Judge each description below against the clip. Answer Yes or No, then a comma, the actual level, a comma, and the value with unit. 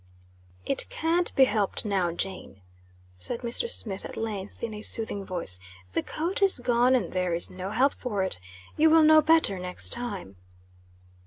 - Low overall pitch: No, high, 220 Hz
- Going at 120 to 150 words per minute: No, average, 170 wpm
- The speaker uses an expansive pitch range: Yes, wide, 6.5 semitones